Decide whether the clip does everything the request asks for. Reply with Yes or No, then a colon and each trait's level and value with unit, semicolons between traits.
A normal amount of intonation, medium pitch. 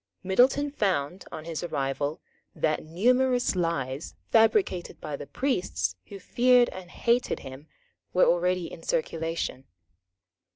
No: wide, 7.8 semitones; medium, 180 Hz